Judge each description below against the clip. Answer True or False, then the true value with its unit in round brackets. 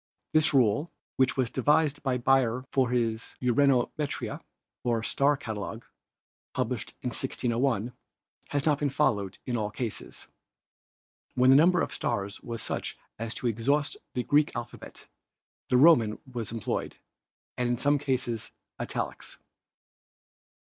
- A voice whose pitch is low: True (125 Hz)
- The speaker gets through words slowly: True (130 wpm)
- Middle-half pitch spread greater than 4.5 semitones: False (3.6 semitones)